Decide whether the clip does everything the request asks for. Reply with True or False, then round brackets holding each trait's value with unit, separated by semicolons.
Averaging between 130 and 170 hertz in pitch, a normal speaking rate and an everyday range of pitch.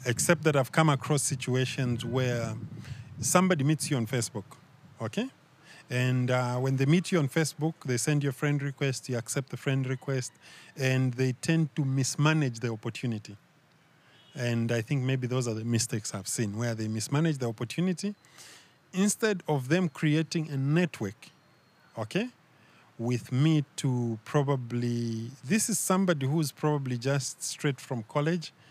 True (135 Hz; 155 wpm; 4.2 semitones)